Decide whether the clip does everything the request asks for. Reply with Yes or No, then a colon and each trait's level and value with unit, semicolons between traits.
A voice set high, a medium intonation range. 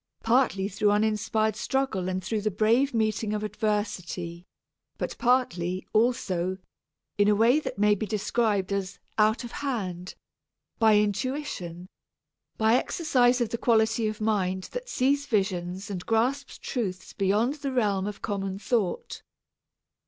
Yes: high, 215 Hz; average, 3.8 semitones